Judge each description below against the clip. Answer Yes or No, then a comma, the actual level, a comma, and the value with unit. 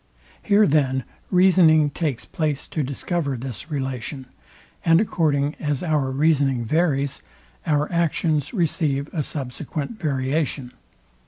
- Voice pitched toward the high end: No, medium, 150 Hz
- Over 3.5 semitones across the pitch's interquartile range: No, average, 3.1 semitones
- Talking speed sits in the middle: No, slow, 110 wpm